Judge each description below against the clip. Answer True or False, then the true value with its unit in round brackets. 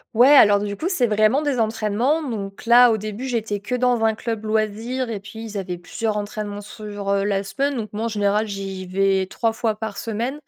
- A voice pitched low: False (215 Hz)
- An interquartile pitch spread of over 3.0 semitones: False (2.5 semitones)